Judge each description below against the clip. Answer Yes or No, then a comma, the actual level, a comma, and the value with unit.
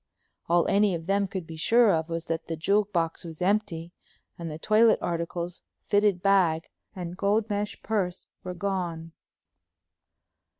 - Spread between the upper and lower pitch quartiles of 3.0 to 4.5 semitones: Yes, average, 3.5 semitones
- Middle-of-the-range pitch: Yes, medium, 180 Hz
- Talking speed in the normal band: Yes, average, 155 wpm